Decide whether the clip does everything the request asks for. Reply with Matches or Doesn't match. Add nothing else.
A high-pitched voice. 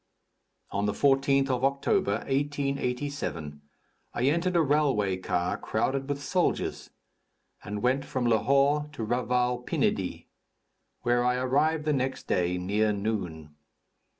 Doesn't match